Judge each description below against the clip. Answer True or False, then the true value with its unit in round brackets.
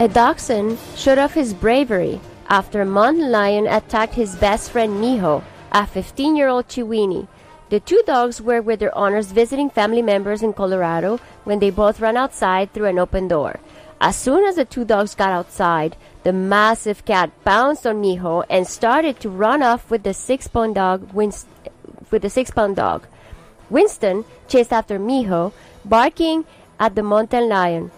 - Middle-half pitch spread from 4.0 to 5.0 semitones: False (3.5 semitones)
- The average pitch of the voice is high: True (215 Hz)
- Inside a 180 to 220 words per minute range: False (165 wpm)